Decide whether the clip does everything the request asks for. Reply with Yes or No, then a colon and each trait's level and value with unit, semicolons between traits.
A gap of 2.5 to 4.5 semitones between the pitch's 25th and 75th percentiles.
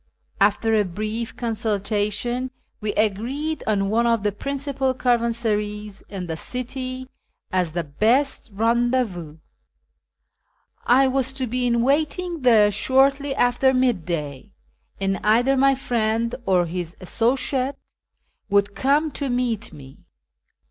Yes: average, 4.1 semitones